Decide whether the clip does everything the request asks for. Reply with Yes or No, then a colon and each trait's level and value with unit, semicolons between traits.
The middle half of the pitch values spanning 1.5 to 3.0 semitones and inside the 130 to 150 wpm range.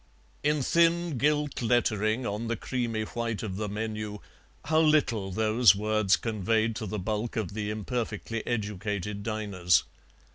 Yes: narrow, 2.5 semitones; average, 140 wpm